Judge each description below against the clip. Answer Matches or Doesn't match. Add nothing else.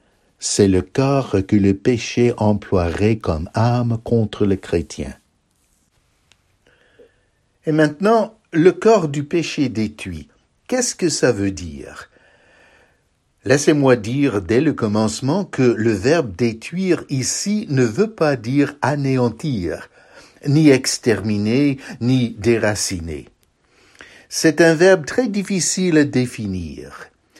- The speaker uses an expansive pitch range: Matches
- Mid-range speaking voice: Doesn't match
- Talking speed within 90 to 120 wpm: Matches